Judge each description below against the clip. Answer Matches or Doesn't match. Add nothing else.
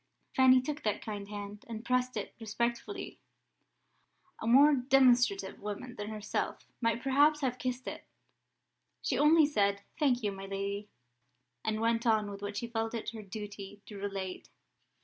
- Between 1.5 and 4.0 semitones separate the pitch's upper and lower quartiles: Matches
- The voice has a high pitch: Matches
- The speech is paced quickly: Doesn't match